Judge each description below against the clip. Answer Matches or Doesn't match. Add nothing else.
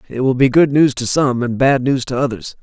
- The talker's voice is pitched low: Matches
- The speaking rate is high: Matches